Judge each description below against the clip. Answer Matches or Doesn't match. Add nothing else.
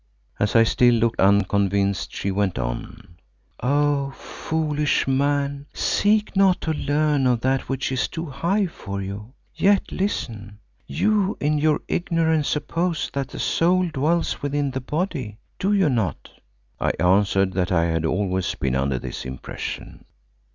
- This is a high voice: Doesn't match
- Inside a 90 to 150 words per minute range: Matches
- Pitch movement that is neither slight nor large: Doesn't match